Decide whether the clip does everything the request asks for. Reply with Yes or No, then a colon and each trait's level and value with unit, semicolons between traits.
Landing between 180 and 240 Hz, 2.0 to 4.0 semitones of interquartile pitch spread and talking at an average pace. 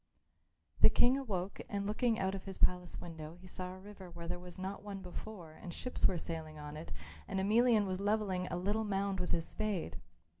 No: high, 190 Hz; average, 2.7 semitones; fast, 210 wpm